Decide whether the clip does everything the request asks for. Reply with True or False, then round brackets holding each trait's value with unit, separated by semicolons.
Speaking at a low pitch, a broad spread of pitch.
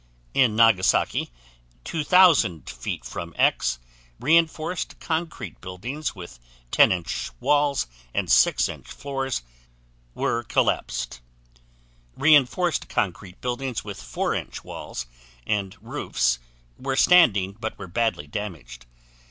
True (115 Hz; 8.4 semitones)